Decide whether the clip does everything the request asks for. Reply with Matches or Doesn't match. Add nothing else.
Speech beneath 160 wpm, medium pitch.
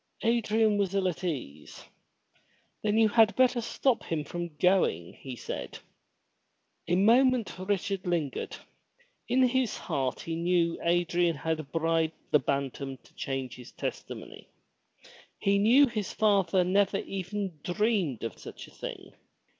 Matches